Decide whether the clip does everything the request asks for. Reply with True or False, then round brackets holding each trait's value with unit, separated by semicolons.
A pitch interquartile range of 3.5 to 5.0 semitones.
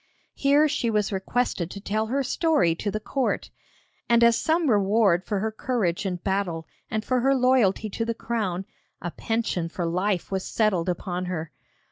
True (4.5 semitones)